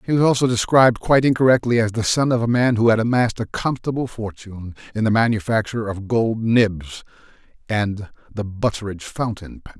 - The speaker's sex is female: No, male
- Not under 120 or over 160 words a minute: No, average, 180 wpm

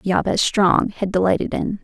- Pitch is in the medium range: No, high, 195 Hz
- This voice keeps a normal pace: Yes, average, 165 wpm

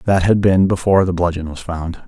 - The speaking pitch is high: No, very low, 90 Hz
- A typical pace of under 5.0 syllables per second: No, 5.7 syllables/s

